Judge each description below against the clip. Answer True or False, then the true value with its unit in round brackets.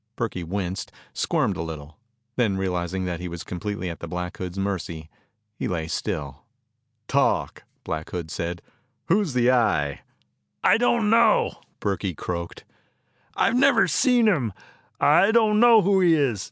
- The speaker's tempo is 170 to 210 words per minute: False (155 wpm)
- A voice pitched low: True (95 Hz)